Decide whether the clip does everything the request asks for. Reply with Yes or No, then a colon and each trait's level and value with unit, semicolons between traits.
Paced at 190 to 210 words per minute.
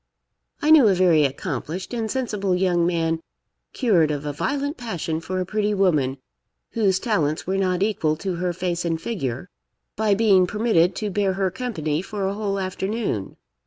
No: average, 170 wpm